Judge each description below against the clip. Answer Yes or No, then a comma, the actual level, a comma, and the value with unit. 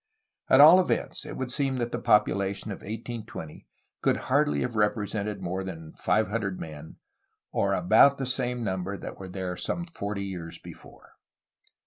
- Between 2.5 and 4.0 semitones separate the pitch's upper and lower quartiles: No, average, 4.4 semitones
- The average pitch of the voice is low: Yes, low, 105 Hz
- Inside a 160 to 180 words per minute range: Yes, average, 165 wpm